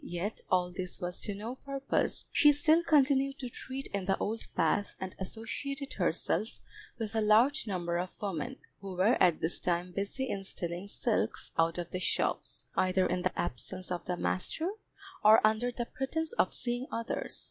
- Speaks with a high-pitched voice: Yes, high, 205 Hz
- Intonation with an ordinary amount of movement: No, wide, 6.2 semitones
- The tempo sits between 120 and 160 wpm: No, average, 180 wpm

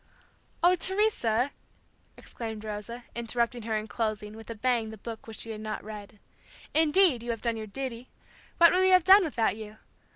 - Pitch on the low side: No, high, 230 Hz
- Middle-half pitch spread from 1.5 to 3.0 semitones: No, average, 4.6 semitones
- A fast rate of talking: No, average, 185 wpm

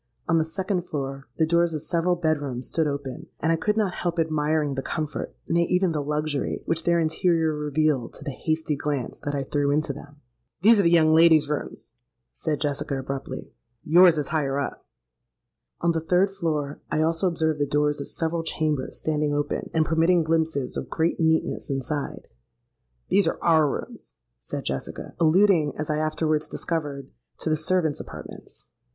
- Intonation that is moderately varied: No, narrow, 2.2 semitones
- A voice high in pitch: No, medium, 155 Hz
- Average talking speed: Yes, average, 175 wpm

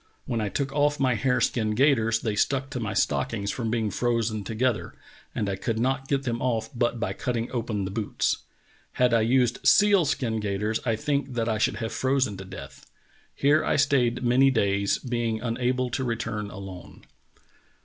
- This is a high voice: No, low, 120 Hz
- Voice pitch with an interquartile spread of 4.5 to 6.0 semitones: No, average, 3.0 semitones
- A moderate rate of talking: Yes, average, 185 wpm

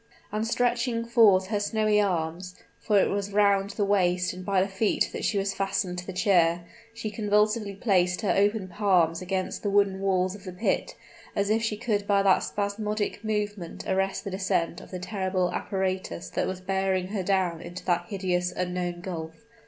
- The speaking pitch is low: No, high, 195 Hz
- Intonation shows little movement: Yes, narrow, 2.2 semitones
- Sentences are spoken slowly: No, average, 185 wpm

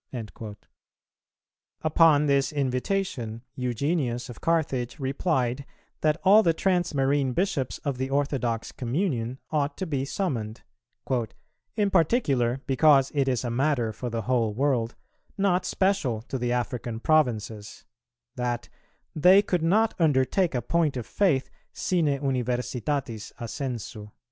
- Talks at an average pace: No, slow, 125 wpm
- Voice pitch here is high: No, low, 135 Hz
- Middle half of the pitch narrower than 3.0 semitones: No, average, 4.6 semitones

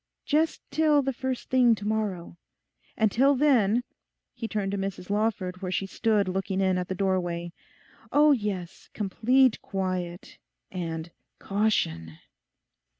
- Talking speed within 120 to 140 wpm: Yes, slow, 135 wpm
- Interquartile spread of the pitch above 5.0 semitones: No, average, 4.7 semitones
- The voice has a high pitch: Yes, high, 200 Hz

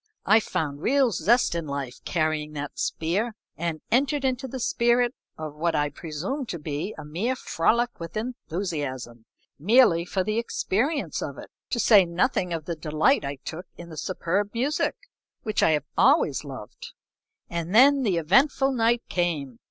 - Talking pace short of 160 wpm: No, average, 165 wpm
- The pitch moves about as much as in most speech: No, wide, 7.4 semitones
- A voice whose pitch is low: No, medium, 175 Hz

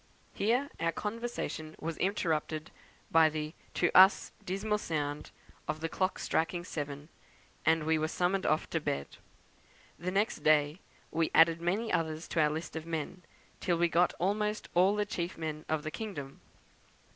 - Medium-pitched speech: Yes, medium, 165 Hz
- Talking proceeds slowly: No, average, 160 wpm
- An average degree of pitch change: Yes, average, 3.4 semitones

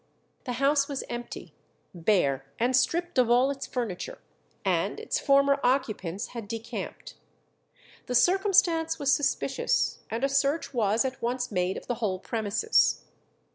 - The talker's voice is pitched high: Yes, very high, 250 Hz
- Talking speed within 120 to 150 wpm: Yes, average, 140 wpm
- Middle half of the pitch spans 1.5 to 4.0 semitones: No, average, 4.4 semitones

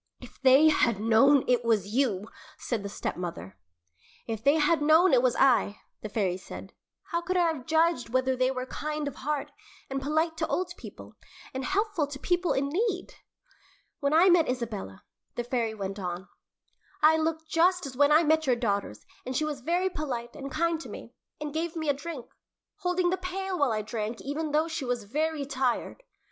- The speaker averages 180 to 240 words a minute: Yes, average, 195 wpm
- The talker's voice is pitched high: Yes, very high, 280 Hz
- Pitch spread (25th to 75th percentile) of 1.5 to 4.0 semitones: No, average, 5.2 semitones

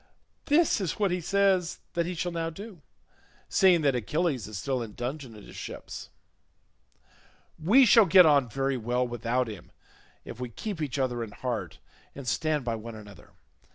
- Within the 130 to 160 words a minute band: No, average, 175 wpm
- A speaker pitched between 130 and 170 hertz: Yes, medium, 140 Hz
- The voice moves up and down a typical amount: No, wide, 6.8 semitones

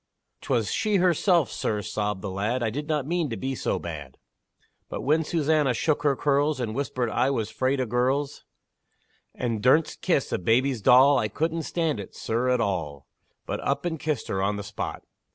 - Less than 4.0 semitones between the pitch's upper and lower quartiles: No, wide, 5.6 semitones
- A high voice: No, low, 130 Hz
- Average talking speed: Yes, average, 190 wpm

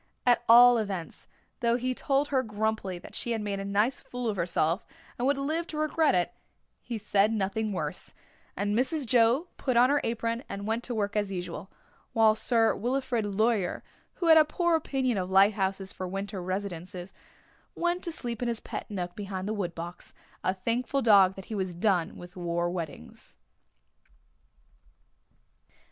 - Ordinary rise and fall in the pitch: Yes, average, 4.4 semitones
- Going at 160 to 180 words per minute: Yes, average, 170 wpm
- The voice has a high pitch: Yes, high, 215 Hz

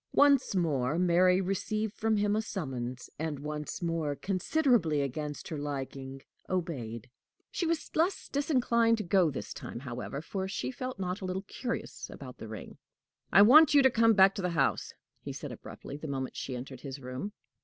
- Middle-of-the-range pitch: Yes, medium, 175 Hz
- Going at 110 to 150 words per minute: No, average, 180 wpm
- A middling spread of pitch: No, wide, 7.7 semitones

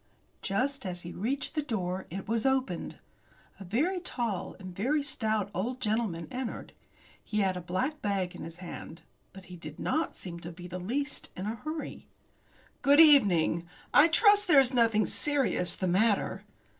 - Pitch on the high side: Yes, high, 215 Hz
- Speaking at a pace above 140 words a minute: Yes, average, 170 wpm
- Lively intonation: Yes, wide, 7.0 semitones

